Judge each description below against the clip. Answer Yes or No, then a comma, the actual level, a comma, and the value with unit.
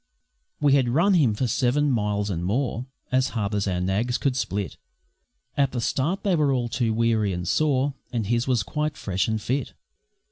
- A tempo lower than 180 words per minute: No, average, 190 wpm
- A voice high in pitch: No, low, 120 Hz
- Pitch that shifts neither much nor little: Yes, average, 4.8 semitones